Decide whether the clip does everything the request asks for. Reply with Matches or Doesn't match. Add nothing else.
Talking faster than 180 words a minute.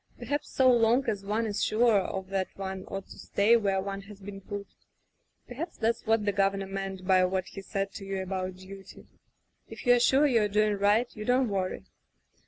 Matches